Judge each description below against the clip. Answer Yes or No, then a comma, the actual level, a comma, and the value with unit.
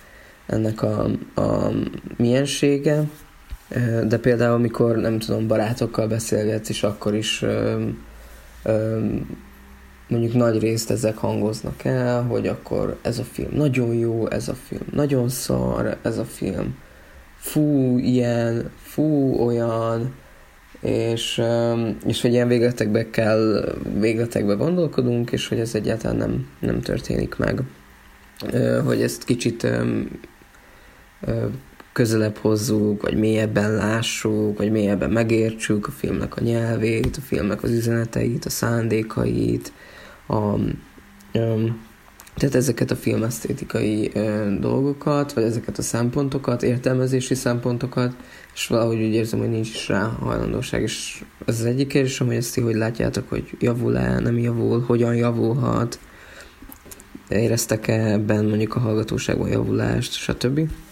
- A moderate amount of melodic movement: No, narrow, 2.2 semitones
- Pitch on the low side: Yes, low, 115 Hz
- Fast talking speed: No, average, 125 wpm